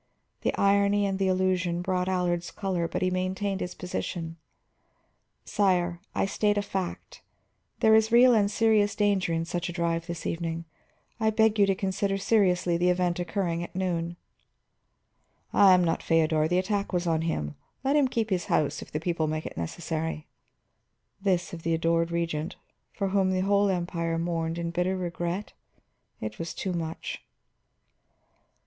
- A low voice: No, medium, 180 Hz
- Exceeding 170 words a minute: No, average, 165 wpm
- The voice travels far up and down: No, average, 2.8 semitones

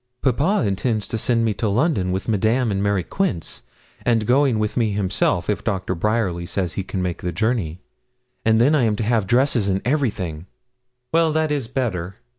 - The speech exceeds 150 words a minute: Yes, average, 185 wpm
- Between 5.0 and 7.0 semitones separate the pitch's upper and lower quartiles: No, average, 4.4 semitones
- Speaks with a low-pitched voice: Yes, low, 110 Hz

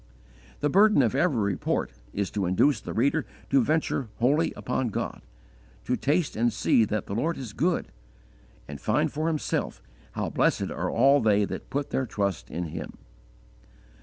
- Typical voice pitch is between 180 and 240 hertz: No, low, 125 Hz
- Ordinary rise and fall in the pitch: No, wide, 6.0 semitones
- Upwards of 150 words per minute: Yes, average, 165 wpm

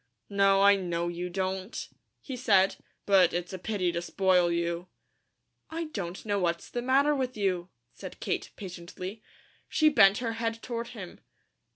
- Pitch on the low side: No, high, 195 Hz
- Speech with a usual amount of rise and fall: Yes, average, 4.3 semitones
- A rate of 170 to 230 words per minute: No, average, 160 wpm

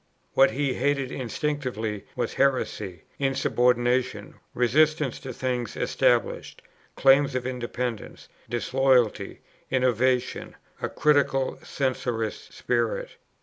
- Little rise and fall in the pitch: Yes, narrow, 2.0 semitones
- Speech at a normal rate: No, slow, 90 wpm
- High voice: No, low, 130 Hz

